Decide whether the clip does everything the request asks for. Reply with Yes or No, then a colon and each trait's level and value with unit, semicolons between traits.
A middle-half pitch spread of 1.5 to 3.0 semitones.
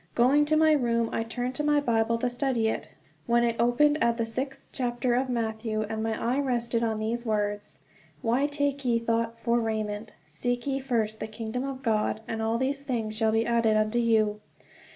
Yes: narrow, 2.5 semitones